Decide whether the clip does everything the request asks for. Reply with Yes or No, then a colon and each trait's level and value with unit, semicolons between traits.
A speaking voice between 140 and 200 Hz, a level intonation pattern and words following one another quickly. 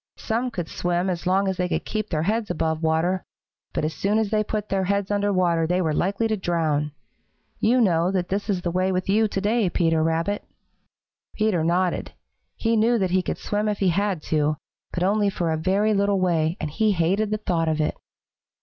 No: medium, 185 Hz; average, 3.6 semitones; fast, 215 wpm